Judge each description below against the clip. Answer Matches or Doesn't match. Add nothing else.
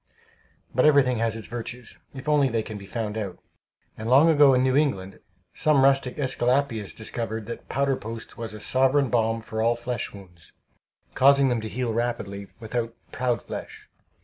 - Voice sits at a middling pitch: Doesn't match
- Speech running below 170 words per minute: Doesn't match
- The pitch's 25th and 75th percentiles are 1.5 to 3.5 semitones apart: Matches